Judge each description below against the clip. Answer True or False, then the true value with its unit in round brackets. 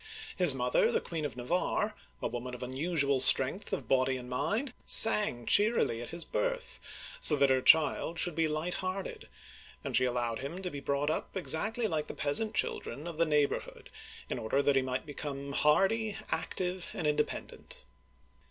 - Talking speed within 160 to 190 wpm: True (180 wpm)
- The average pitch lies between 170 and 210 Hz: False (150 Hz)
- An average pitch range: False (5.7 semitones)